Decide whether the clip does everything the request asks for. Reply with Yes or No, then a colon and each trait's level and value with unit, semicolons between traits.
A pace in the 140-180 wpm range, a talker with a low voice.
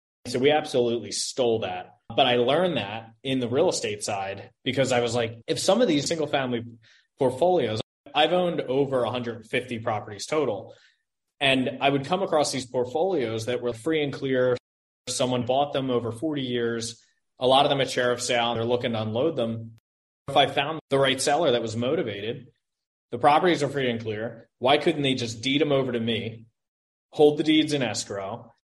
No: average, 190 wpm; low, 125 Hz